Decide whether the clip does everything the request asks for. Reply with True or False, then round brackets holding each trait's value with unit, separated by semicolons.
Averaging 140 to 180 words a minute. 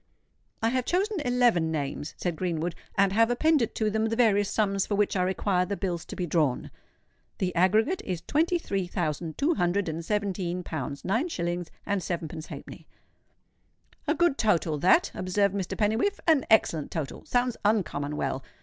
True (165 wpm)